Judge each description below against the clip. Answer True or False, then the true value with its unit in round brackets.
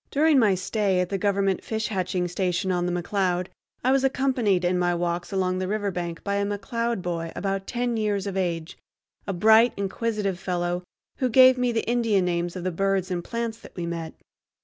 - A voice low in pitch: False (195 Hz)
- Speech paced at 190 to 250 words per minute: True (195 wpm)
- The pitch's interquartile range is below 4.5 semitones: True (3.7 semitones)